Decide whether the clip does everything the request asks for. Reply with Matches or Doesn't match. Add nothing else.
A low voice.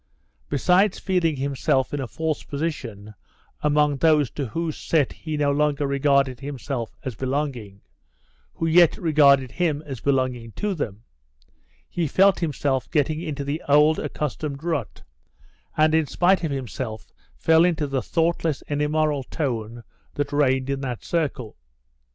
Doesn't match